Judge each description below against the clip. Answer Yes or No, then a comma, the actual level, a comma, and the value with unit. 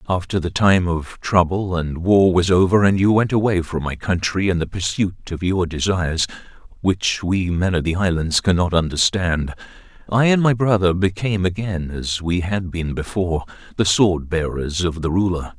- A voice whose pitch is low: Yes, very low, 90 Hz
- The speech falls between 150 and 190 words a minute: Yes, average, 180 wpm